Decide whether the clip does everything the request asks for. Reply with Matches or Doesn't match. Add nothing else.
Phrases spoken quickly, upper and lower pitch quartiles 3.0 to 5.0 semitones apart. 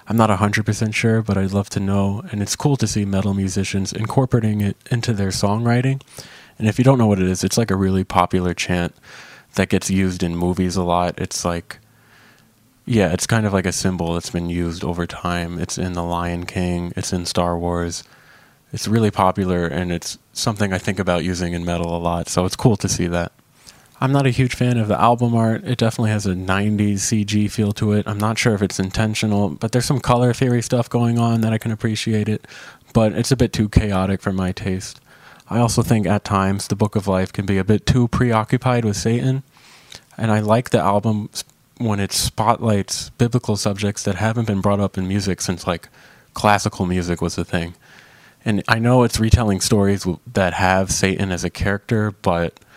Matches